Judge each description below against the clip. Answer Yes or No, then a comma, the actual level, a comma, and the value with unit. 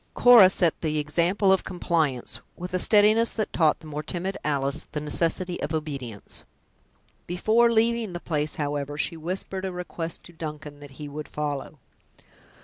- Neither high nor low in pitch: Yes, medium, 165 Hz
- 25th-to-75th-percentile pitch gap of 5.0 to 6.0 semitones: No, average, 4.0 semitones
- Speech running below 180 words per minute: Yes, average, 160 wpm